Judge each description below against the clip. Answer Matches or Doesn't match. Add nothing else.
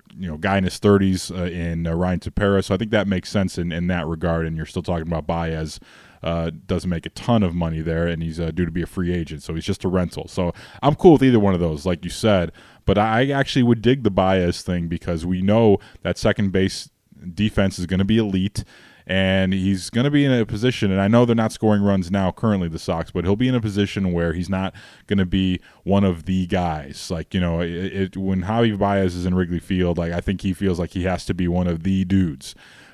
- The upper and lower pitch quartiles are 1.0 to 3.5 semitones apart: Matches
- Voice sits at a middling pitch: Doesn't match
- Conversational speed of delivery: Doesn't match